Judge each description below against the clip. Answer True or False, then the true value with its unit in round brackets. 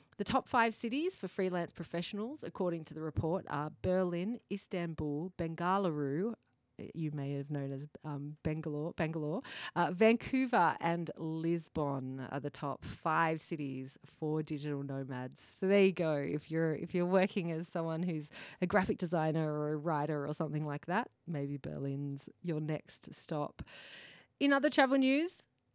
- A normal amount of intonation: True (4.2 semitones)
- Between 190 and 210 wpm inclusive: False (155 wpm)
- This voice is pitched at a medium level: True (165 Hz)